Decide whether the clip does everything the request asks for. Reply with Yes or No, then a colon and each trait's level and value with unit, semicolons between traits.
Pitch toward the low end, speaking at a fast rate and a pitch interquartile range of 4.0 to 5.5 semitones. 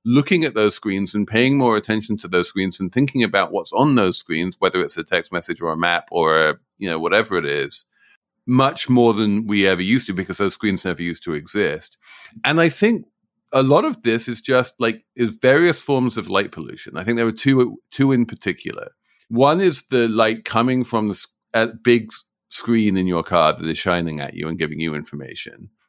Yes: low, 115 Hz; fast, 210 wpm; average, 4.6 semitones